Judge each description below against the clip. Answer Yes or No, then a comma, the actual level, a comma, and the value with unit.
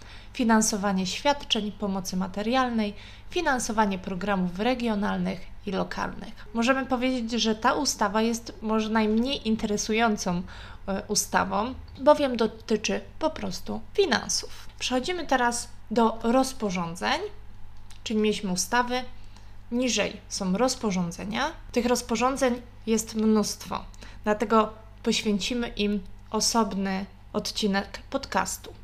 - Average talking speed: No, slow, 90 wpm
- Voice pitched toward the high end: Yes, high, 220 Hz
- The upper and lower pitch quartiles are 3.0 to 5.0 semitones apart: Yes, average, 3.4 semitones